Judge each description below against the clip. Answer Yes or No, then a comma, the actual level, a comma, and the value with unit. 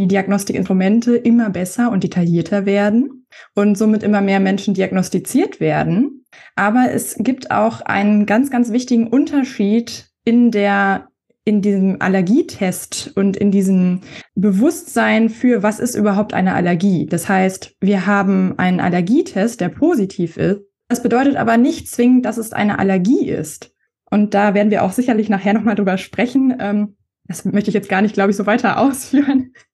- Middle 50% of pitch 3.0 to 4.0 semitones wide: Yes, average, 3.7 semitones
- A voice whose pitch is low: No, high, 205 Hz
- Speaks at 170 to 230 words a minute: No, average, 155 wpm